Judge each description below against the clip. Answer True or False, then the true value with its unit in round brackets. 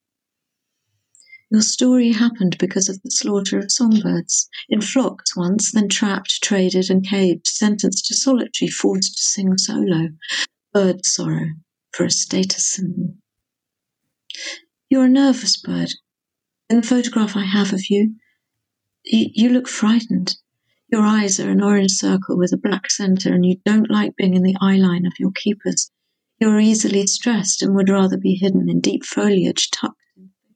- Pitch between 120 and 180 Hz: False (200 Hz)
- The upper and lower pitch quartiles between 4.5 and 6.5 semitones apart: False (3.0 semitones)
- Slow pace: False (155 wpm)